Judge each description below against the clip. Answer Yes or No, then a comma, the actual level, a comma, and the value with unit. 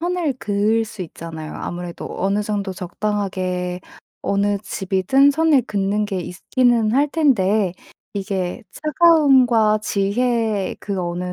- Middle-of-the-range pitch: No, high, 205 Hz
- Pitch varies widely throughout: No, average, 4.7 semitones